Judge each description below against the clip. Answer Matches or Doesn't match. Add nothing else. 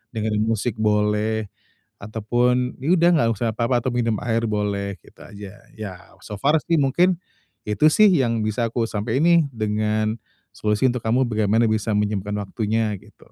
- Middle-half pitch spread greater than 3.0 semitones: Doesn't match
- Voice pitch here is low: Matches